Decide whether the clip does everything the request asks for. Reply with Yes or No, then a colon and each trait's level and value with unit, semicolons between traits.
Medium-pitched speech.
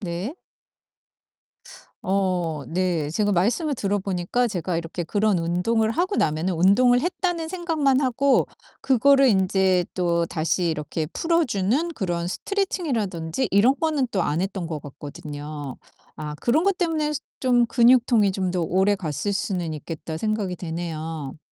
No: high, 195 Hz